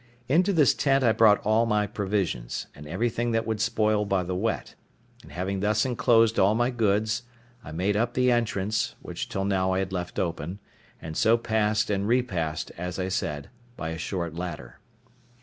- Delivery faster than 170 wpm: Yes, average, 185 wpm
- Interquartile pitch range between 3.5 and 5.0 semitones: Yes, average, 3.9 semitones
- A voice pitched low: Yes, low, 105 Hz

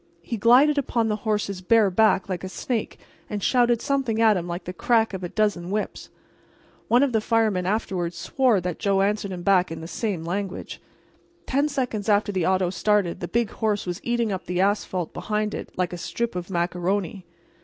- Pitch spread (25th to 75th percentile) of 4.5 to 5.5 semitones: No, average, 3.9 semitones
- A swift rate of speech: No, average, 195 wpm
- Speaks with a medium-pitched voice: No, high, 205 Hz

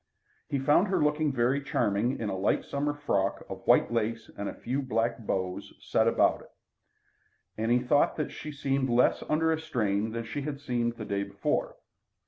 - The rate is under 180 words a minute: No, average, 190 wpm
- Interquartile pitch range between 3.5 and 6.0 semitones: Yes, average, 4.8 semitones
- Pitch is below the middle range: Yes, low, 120 Hz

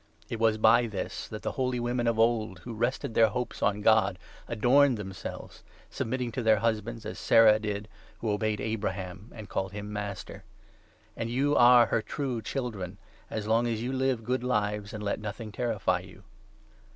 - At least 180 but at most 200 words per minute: Yes, average, 190 wpm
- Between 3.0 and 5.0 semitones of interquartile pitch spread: No, narrow, 2.6 semitones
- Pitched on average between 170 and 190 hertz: No, low, 110 Hz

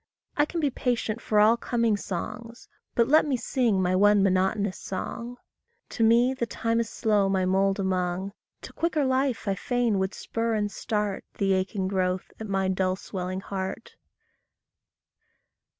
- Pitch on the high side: Yes, high, 210 Hz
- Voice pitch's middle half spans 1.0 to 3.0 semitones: No, average, 3.6 semitones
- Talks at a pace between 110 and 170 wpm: Yes, average, 160 wpm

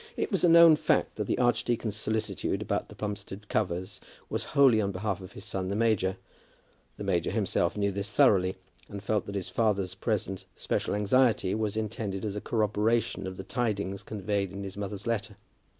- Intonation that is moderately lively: No, narrow, 2.2 semitones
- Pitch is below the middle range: Yes, low, 105 Hz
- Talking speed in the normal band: Yes, average, 185 wpm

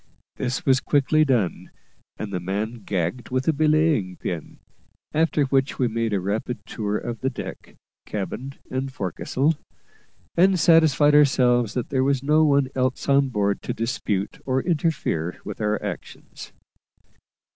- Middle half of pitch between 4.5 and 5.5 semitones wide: Yes, average, 5.2 semitones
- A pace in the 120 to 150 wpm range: Yes, average, 145 wpm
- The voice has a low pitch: Yes, low, 130 Hz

